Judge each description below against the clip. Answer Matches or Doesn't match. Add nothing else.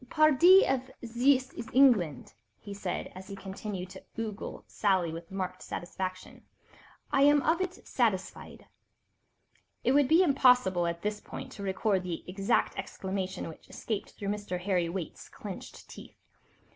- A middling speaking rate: Matches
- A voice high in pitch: Matches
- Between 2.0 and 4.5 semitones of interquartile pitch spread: Doesn't match